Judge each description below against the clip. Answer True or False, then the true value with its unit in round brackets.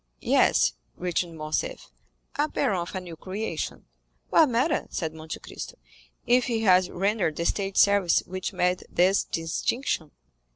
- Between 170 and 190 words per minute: False (140 wpm)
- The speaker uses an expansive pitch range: False (4.1 semitones)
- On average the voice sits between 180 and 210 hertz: True (185 Hz)